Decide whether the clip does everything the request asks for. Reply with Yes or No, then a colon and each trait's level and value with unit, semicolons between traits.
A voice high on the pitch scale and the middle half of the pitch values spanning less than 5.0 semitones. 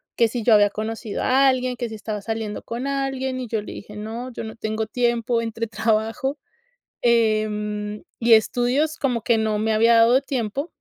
Yes: high, 230 Hz; narrow, 2.5 semitones